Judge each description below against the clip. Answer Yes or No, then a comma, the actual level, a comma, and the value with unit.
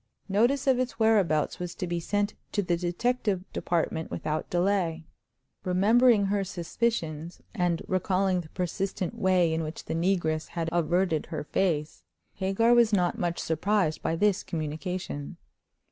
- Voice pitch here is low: No, medium, 180 Hz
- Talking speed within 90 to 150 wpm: Yes, average, 145 wpm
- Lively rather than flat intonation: No, average, 3.7 semitones